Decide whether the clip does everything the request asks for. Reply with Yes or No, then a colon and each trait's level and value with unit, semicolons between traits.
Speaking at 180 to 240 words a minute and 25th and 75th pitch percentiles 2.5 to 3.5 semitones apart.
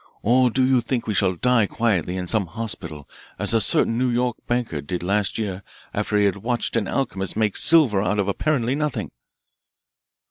No: average, 185 wpm; average, 4.2 semitones